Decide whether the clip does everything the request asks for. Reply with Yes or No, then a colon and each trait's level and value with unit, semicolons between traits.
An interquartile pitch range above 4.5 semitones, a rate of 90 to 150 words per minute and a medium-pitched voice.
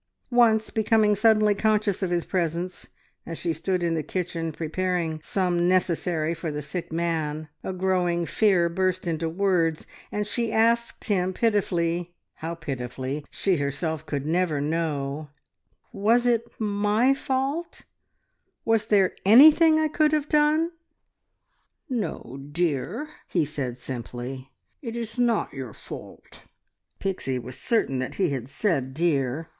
Yes: wide, 5.6 semitones; slow, 135 wpm; medium, 175 Hz